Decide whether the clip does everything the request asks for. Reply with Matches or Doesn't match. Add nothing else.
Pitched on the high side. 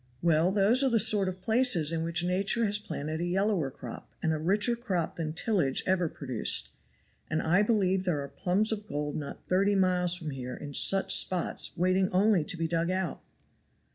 Doesn't match